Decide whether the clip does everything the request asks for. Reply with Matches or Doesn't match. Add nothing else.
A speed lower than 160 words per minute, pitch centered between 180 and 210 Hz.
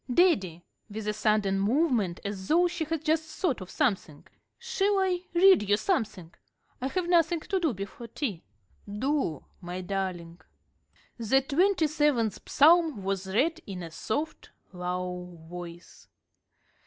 Doesn't match